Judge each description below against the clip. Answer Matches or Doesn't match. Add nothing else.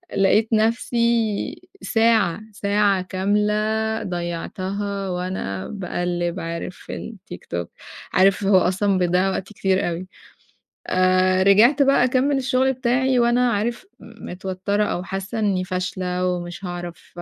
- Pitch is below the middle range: Doesn't match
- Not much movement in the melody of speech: Doesn't match